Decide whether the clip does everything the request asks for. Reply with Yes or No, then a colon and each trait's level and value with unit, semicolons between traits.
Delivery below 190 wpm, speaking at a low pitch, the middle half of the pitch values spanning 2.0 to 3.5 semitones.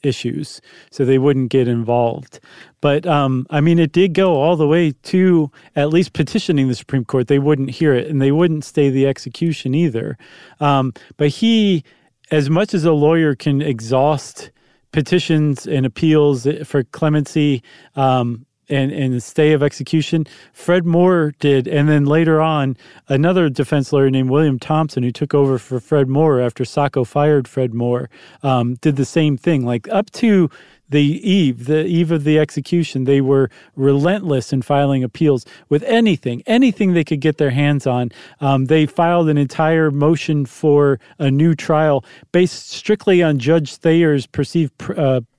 No: average, 170 wpm; medium, 145 Hz; average, 3.1 semitones